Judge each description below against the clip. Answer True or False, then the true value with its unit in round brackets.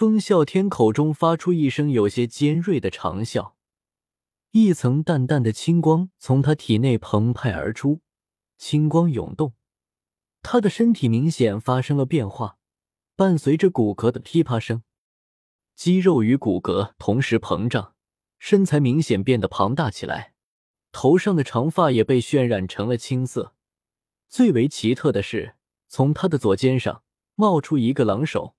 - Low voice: True (130 Hz)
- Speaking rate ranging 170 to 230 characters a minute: True (220 characters per minute)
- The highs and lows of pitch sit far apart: True (6.6 semitones)